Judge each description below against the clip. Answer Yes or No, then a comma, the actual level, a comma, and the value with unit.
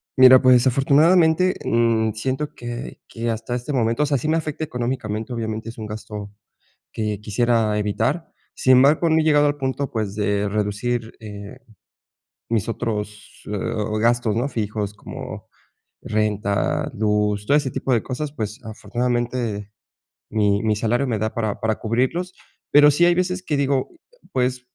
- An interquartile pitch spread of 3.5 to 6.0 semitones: Yes, average, 4.2 semitones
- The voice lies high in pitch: No, low, 120 Hz